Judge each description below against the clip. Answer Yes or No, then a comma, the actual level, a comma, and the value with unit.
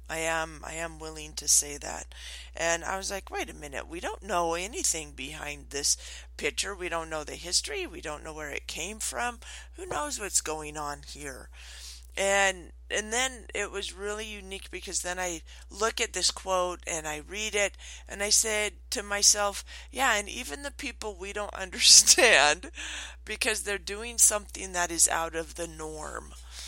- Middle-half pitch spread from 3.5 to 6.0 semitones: Yes, average, 5.1 semitones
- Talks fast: No, average, 180 wpm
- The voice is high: No, medium, 180 Hz